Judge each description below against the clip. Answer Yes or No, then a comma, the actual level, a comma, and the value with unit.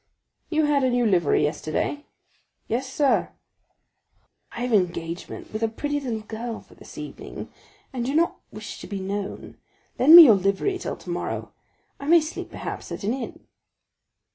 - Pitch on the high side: Yes, high, 240 Hz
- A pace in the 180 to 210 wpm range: No, average, 165 wpm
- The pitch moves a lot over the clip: Yes, wide, 6.3 semitones